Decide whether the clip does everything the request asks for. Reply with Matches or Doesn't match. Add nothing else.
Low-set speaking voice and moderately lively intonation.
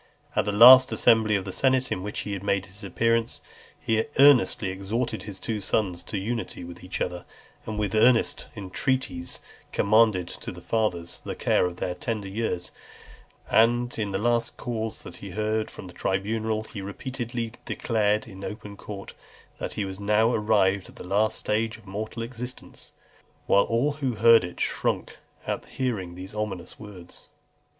Matches